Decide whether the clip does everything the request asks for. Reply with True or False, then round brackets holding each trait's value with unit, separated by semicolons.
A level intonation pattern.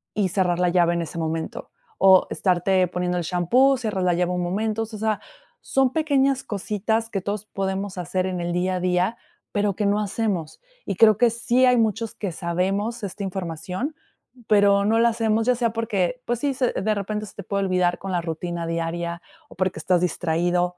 False (3.8 semitones)